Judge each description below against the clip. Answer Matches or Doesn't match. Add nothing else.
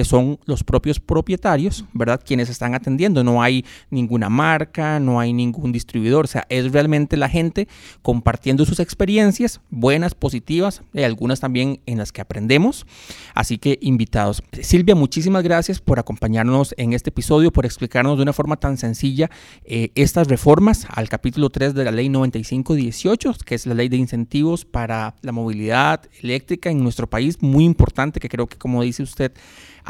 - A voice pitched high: Doesn't match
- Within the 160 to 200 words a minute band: Matches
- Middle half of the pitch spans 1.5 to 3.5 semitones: Doesn't match